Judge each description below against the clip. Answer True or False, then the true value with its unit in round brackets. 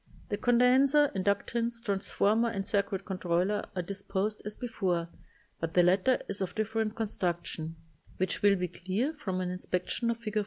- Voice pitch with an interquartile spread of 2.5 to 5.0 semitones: True (3.7 semitones)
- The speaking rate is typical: True (165 wpm)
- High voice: True (200 Hz)